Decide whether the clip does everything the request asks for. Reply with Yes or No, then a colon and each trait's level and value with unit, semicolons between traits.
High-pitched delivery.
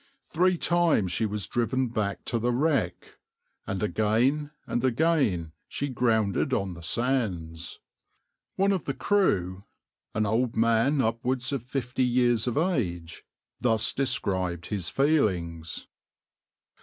No: low, 115 Hz